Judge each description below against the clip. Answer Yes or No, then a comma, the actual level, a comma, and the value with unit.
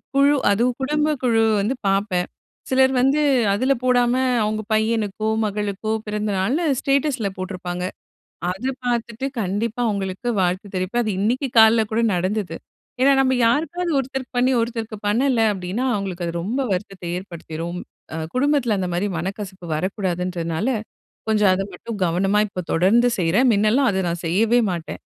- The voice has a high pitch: Yes, high, 215 Hz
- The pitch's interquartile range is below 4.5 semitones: No, average, 4.8 semitones